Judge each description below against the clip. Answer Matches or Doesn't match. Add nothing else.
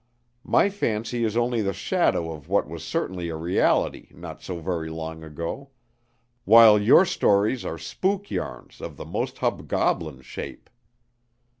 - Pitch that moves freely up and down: Matches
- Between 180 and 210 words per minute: Doesn't match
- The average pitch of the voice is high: Doesn't match